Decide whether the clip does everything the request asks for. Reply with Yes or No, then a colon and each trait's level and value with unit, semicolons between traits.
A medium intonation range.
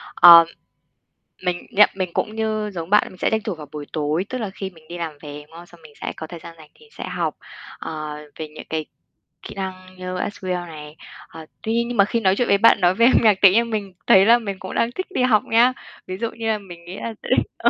Yes: average, 4.8 semitones